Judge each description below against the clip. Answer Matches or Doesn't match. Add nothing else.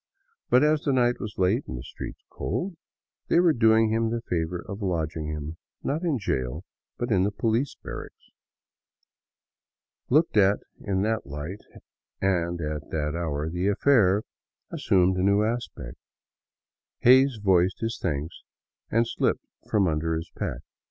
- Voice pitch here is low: Matches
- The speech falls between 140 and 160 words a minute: Matches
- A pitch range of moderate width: Doesn't match